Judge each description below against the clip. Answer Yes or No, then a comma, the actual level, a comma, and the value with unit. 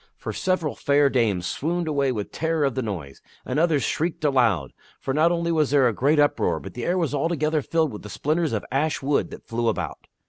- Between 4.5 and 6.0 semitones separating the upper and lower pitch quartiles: Yes, average, 5.0 semitones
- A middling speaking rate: No, fast, 220 wpm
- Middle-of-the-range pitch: Yes, medium, 145 Hz